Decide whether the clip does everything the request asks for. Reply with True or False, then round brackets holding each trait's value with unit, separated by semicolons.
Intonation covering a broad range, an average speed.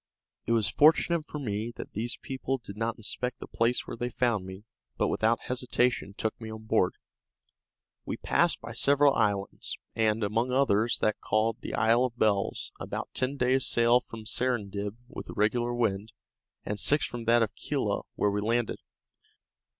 False (2.7 semitones; 175 wpm)